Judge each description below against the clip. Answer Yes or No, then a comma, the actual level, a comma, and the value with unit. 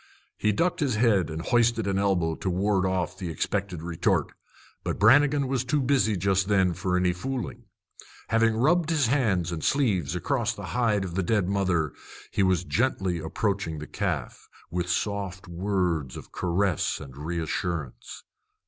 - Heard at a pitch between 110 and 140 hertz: No, very low, 95 Hz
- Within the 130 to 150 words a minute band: No, average, 160 wpm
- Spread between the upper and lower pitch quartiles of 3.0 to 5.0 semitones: Yes, average, 4.5 semitones